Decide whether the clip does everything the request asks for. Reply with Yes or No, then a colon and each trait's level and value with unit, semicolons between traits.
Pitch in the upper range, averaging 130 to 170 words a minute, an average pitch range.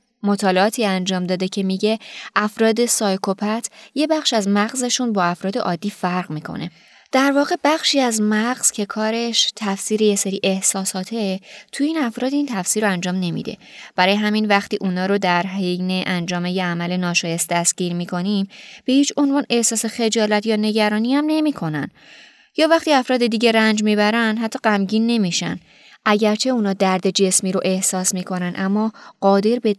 Yes: high, 210 Hz; fast, 155 wpm; average, 3.7 semitones